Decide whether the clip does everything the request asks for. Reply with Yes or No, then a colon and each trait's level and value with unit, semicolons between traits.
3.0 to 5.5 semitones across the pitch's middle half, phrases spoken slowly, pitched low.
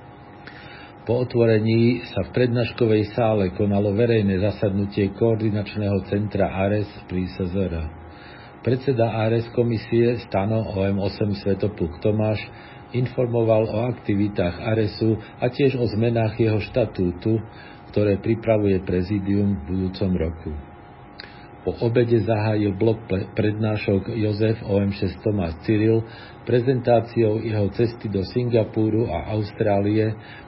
No: narrow, 2.5 semitones; slow, 100 wpm; low, 110 Hz